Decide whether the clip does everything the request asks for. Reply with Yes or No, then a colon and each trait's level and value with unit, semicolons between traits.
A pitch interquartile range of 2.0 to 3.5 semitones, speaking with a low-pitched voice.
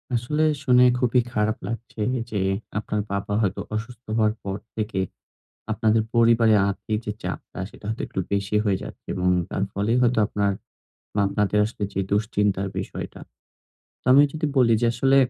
Yes: narrow, 2.5 semitones; low, 110 Hz